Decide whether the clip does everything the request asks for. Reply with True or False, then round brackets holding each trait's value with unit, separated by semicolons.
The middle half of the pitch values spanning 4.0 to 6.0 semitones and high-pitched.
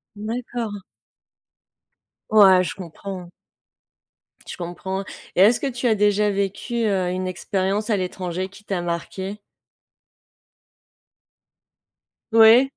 False (2.8 semitones; 200 Hz)